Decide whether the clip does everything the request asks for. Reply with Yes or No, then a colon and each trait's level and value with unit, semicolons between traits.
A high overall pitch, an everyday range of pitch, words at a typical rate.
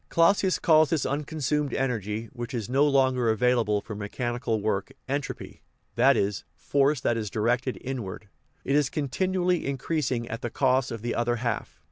No: low, 125 Hz; average, 3.6 semitones; average, 165 wpm